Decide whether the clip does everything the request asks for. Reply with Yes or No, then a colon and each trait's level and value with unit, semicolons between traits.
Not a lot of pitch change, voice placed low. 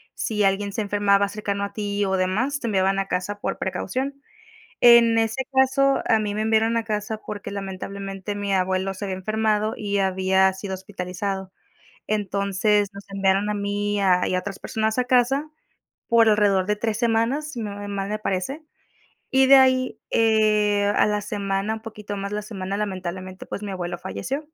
No: narrow, 2.3 semitones; high, 205 Hz